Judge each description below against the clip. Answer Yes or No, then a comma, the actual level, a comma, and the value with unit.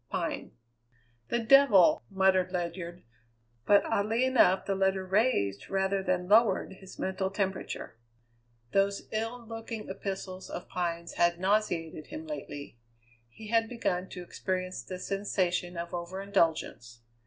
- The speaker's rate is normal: No, slow, 130 wpm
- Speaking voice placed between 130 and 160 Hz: No, high, 190 Hz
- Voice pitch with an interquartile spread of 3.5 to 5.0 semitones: No, average, 2.8 semitones